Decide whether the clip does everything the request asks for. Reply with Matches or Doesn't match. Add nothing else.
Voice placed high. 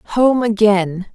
Matches